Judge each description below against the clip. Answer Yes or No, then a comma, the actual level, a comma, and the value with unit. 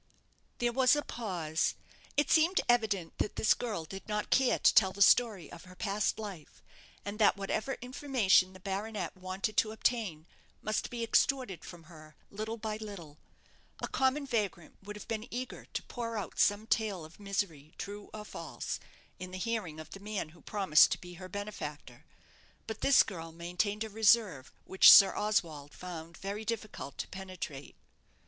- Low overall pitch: No, high, 200 Hz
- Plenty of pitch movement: No, average, 3.8 semitones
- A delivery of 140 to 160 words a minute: No, average, 175 wpm